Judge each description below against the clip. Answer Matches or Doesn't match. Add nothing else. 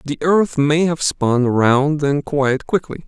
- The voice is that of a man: Matches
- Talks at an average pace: Matches